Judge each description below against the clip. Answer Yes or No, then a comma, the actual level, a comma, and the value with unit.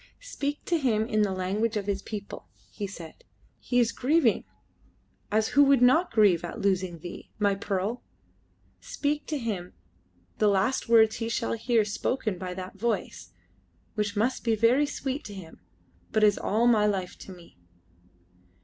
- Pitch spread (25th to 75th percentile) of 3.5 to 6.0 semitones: Yes, average, 4.0 semitones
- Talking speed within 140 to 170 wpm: Yes, average, 165 wpm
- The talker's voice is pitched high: Yes, high, 215 Hz